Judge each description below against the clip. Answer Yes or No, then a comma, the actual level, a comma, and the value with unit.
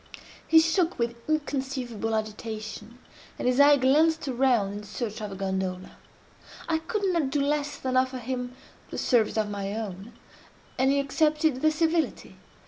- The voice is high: Yes, very high, 255 Hz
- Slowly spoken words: No, average, 155 wpm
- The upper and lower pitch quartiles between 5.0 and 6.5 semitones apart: Yes, wide, 5.5 semitones